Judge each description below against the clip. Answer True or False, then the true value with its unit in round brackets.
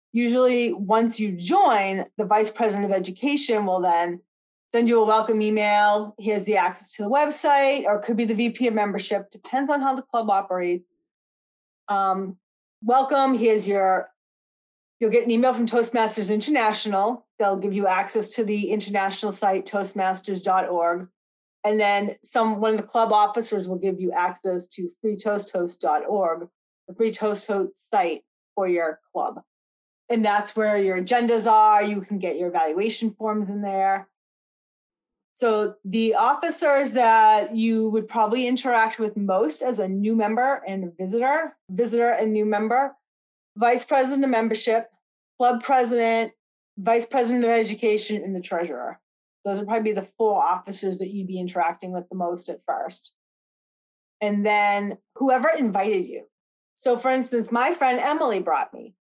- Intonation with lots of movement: False (3.2 semitones)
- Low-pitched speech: False (215 Hz)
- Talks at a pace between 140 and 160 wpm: True (155 wpm)